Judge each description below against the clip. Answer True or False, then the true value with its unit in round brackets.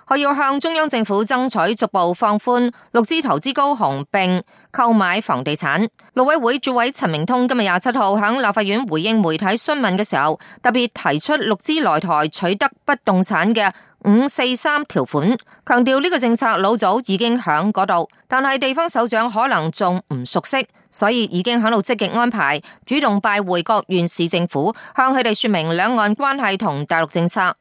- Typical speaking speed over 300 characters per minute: False (280 characters per minute)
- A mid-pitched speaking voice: False (225 Hz)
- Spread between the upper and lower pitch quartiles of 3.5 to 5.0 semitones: False (5.4 semitones)